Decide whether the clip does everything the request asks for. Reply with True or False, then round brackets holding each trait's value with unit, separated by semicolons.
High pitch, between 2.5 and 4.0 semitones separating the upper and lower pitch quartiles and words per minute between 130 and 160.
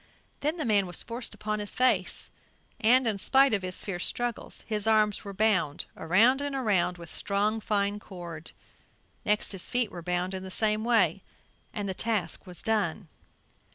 False (210 Hz; 3.4 semitones; 175 wpm)